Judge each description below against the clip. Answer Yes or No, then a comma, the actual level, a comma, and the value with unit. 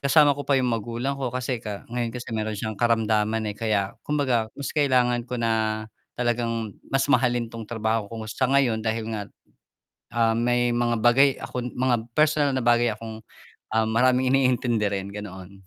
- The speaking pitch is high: No, low, 120 Hz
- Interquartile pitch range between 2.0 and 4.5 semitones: Yes, narrow, 2.5 semitones